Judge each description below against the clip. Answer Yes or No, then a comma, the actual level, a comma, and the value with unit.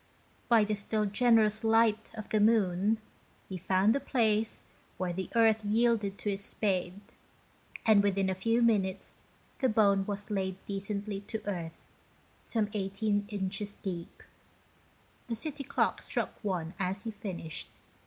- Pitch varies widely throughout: No, narrow, 2.4 semitones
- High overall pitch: Yes, high, 205 Hz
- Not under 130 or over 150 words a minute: Yes, average, 145 wpm